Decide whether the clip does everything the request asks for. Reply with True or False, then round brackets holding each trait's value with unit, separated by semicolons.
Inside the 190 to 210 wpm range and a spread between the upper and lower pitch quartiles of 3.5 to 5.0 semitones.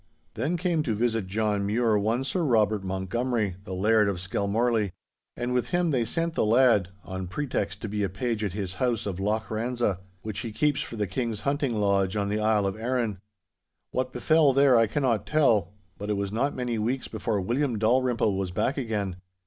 True (195 wpm; 3.8 semitones)